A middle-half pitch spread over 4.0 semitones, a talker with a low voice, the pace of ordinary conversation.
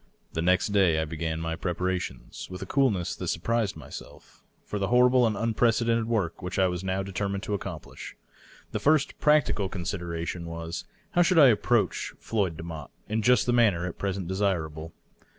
Yes: average, 5.2 semitones; very low, 95 Hz; average, 180 wpm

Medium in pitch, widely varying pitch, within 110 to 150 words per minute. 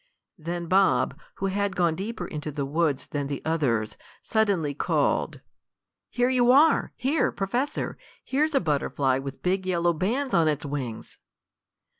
Yes: medium, 175 Hz; wide, 6.9 semitones; average, 145 wpm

